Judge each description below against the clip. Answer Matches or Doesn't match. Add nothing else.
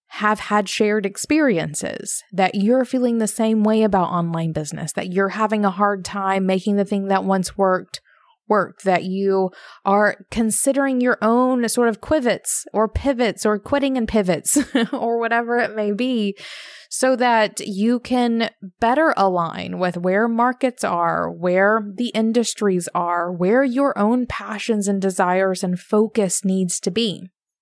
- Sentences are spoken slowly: Doesn't match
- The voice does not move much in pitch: Doesn't match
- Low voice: Doesn't match